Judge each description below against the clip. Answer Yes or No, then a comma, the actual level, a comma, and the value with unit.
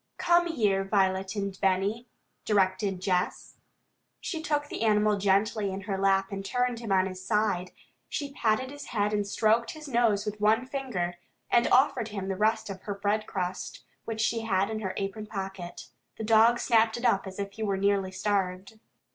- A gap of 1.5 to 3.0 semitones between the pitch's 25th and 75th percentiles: Yes, average, 2.7 semitones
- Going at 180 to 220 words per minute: Yes, average, 185 wpm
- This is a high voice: Yes, high, 205 Hz